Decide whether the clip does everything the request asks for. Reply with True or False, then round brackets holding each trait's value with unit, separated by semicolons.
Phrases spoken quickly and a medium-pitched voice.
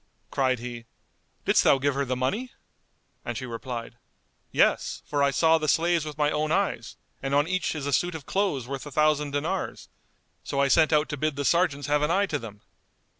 True (210 wpm; 145 Hz)